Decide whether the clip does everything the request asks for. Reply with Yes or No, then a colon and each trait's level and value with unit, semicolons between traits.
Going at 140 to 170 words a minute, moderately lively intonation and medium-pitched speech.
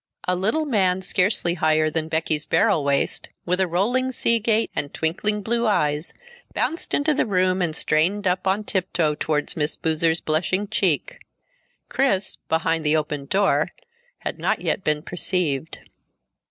Yes: average, 155 wpm; average, 4.7 semitones; medium, 180 Hz